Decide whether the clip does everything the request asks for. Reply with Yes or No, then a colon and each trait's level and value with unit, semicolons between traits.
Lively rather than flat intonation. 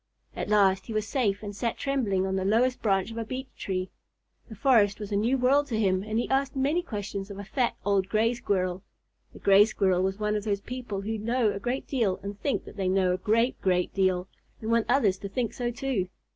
No: average, 3.8 semitones